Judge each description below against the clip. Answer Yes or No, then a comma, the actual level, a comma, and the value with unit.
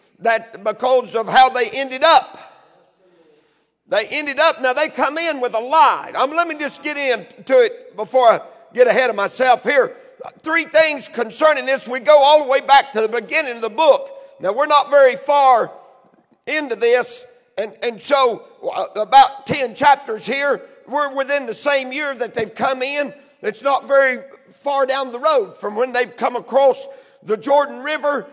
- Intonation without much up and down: No, average, 3.5 semitones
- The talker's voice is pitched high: Yes, very high, 270 Hz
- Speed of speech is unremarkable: Yes, average, 180 wpm